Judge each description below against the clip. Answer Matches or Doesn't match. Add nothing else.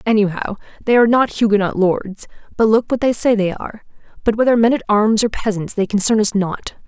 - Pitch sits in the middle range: Doesn't match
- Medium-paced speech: Doesn't match